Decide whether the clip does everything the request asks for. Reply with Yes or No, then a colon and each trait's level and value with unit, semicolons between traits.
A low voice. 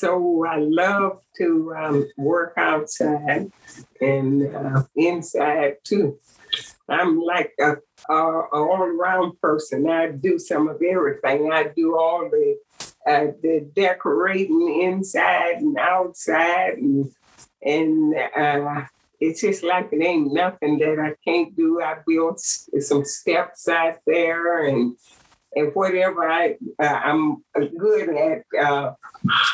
No: medium, 165 Hz